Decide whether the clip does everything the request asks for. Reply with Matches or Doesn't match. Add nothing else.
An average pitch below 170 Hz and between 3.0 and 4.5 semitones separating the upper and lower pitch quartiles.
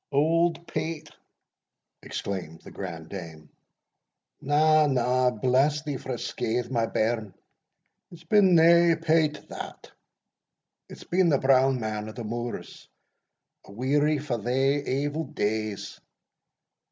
Doesn't match